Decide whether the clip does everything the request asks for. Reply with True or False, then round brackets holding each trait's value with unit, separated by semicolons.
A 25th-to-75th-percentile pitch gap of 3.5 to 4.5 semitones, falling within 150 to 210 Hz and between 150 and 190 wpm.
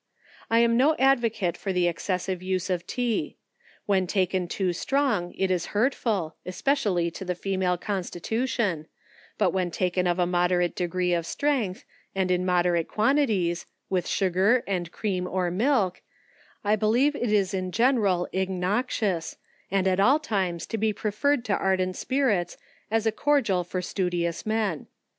True (3.8 semitones; 190 Hz; 160 wpm)